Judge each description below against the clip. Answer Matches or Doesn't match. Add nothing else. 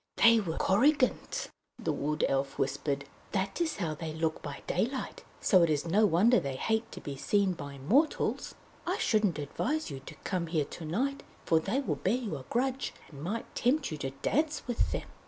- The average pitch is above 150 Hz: Matches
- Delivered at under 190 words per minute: Doesn't match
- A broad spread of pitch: Matches